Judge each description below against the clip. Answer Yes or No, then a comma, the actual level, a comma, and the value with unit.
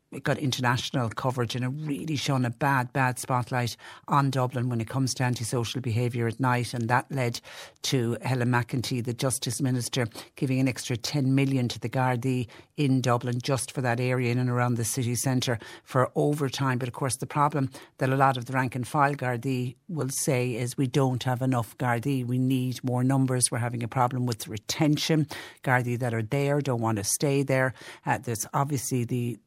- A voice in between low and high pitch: No, low, 125 Hz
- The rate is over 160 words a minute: Yes, average, 200 wpm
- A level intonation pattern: Yes, narrow, 1.9 semitones